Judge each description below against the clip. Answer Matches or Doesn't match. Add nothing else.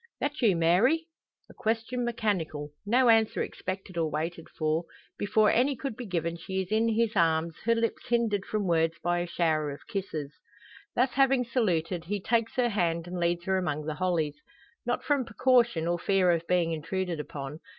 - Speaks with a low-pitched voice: Doesn't match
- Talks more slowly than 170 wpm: Doesn't match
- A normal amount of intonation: Doesn't match